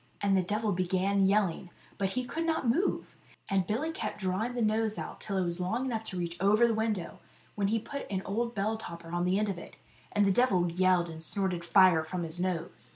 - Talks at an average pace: No, fast, 225 wpm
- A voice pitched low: No, high, 195 Hz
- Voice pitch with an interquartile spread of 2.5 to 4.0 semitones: Yes, average, 3.6 semitones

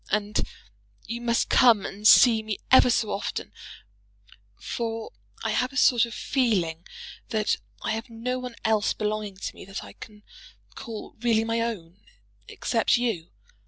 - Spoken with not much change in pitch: Yes, narrow, 2.1 semitones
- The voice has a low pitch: No, high, 225 Hz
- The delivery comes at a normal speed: Yes, average, 155 wpm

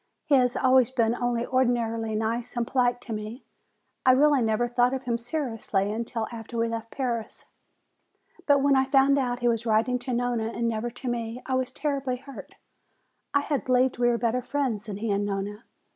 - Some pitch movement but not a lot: No, narrow, 2.3 semitones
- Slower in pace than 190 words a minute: No, average, 195 wpm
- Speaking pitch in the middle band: No, high, 240 Hz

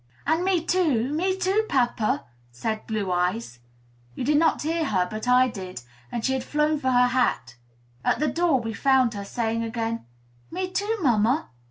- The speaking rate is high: No, average, 180 wpm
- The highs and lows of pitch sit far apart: Yes, wide, 6.1 semitones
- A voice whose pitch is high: Yes, very high, 250 Hz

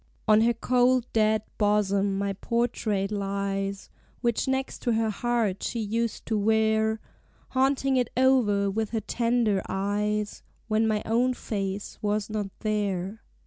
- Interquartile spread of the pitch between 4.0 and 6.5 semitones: No, narrow, 2.6 semitones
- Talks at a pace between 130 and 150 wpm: Yes, average, 140 wpm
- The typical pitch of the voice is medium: No, high, 215 Hz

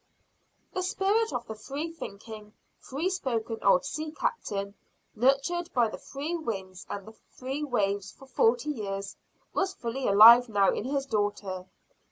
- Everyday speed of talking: Yes, average, 150 wpm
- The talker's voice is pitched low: No, high, 240 Hz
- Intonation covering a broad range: Yes, wide, 6.5 semitones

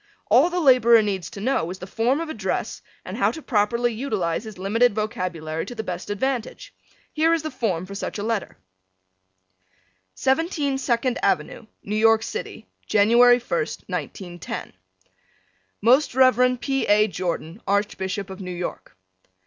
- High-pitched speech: Yes, high, 220 Hz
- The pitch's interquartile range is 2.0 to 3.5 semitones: No, average, 4.8 semitones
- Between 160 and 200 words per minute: No, average, 150 wpm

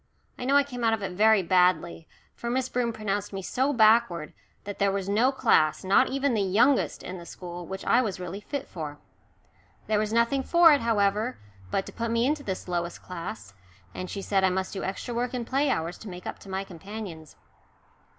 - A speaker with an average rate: No, fast, 215 wpm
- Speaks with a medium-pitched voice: No, high, 205 Hz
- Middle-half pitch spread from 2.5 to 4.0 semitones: No, average, 4.7 semitones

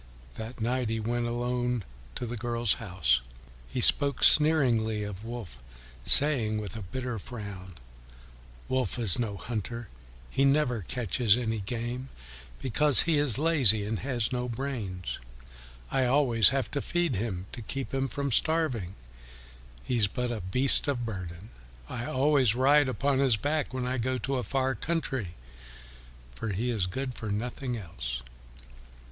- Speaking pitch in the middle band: No, low, 120 Hz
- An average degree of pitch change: Yes, average, 3.8 semitones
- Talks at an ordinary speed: Yes, average, 150 wpm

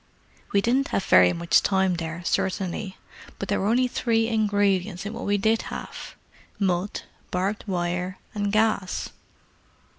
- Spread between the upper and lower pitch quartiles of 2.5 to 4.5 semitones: Yes, average, 2.9 semitones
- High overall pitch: Yes, high, 195 Hz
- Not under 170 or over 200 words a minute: No, average, 140 wpm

